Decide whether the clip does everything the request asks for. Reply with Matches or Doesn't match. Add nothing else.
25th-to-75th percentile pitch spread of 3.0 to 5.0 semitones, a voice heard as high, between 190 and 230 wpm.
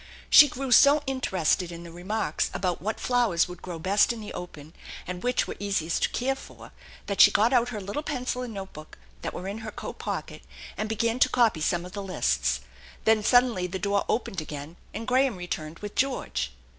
Doesn't match